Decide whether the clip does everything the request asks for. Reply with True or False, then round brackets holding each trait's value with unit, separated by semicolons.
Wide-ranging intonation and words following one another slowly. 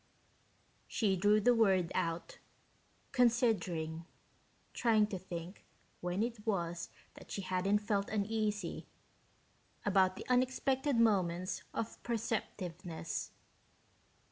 False (4.0 semitones; 95 wpm)